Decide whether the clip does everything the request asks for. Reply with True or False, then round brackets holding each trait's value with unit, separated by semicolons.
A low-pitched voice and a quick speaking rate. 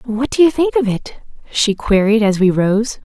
False (230 Hz; 210 wpm)